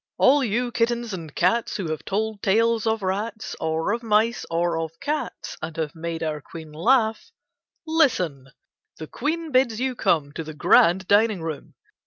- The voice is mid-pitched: No, high, 205 Hz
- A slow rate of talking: No, average, 170 wpm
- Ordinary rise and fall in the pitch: No, wide, 6.2 semitones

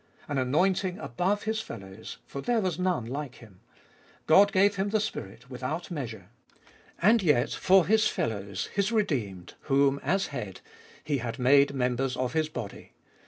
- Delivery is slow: No, average, 160 wpm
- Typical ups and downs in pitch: No, wide, 7.7 semitones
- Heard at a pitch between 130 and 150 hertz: Yes, medium, 140 Hz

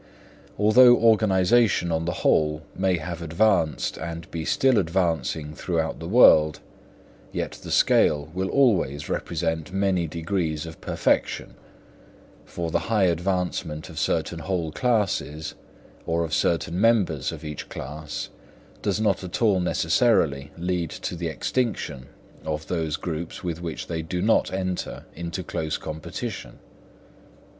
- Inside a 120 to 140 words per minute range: Yes, slow, 135 wpm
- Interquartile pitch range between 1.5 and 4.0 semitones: Yes, average, 3.3 semitones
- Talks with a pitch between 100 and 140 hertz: No, very low, 85 Hz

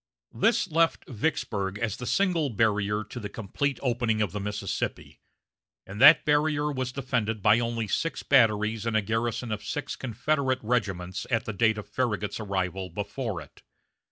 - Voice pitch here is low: Yes, low, 115 Hz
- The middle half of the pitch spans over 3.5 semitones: Yes, average, 4.1 semitones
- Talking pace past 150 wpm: Yes, average, 160 wpm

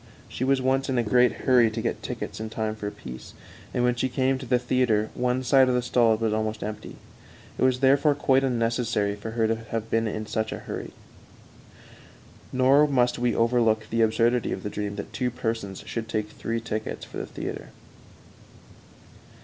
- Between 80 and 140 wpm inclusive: No, average, 195 wpm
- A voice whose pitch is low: Yes, low, 115 Hz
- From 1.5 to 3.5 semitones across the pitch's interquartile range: Yes, narrow, 2.6 semitones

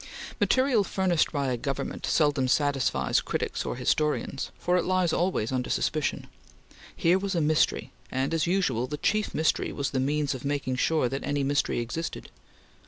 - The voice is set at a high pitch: No, medium, 145 Hz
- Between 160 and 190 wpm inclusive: Yes, average, 170 wpm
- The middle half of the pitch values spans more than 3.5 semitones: Yes, average, 4.4 semitones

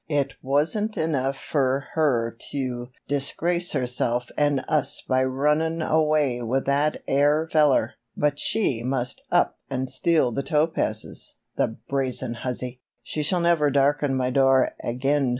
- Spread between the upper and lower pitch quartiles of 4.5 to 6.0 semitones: No, average, 2.8 semitones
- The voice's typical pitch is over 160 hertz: No, medium, 140 Hz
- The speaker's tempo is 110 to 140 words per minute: Yes, slow, 135 wpm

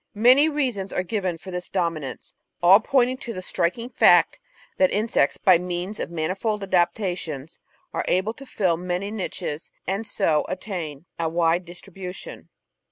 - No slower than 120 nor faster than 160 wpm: Yes, average, 150 wpm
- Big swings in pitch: No, average, 3.5 semitones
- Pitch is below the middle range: No, medium, 185 Hz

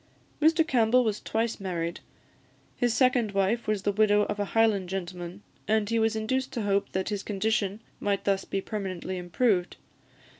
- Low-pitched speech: No, high, 205 Hz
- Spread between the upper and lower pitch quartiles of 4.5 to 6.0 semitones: No, average, 2.7 semitones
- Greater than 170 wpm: No, average, 165 wpm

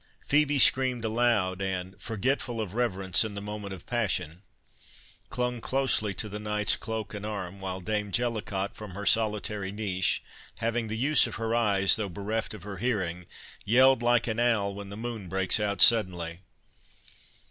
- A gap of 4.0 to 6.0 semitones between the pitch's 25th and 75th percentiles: No, average, 3.1 semitones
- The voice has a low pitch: Yes, low, 105 Hz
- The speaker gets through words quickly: No, average, 165 wpm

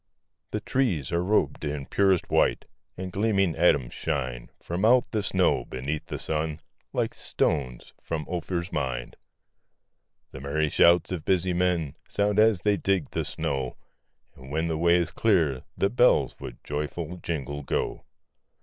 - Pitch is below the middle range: Yes, very low, 85 Hz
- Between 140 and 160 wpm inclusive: Yes, average, 150 wpm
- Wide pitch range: No, average, 4.6 semitones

